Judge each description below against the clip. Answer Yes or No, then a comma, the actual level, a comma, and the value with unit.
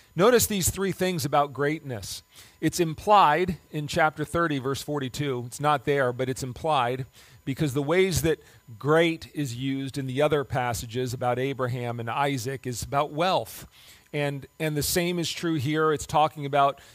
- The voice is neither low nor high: Yes, medium, 145 Hz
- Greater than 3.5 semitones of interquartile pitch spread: No, average, 3.2 semitones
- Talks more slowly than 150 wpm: No, average, 165 wpm